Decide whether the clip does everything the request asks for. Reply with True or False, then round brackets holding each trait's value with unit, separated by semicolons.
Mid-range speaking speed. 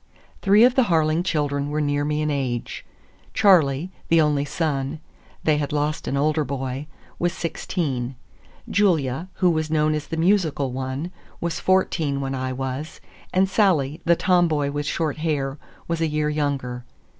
True (155 wpm)